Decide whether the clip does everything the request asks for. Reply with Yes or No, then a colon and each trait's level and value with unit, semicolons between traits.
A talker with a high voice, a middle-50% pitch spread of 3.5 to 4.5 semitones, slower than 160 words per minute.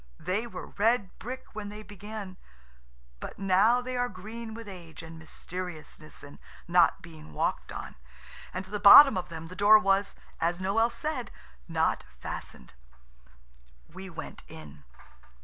Yes: high, 195 Hz; average, 4.2 semitones; average, 150 wpm